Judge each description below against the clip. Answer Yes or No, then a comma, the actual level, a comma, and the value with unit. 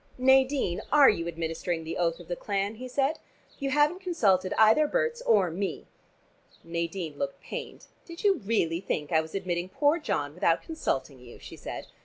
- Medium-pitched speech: No, high, 195 Hz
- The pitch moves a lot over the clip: Yes, wide, 9.0 semitones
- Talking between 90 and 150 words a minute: No, average, 175 wpm